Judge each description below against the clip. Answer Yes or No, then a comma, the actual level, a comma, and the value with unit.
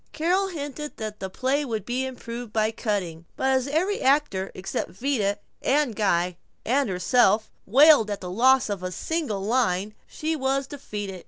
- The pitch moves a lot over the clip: Yes, wide, 5.8 semitones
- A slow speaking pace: No, average, 165 wpm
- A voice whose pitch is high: Yes, high, 235 Hz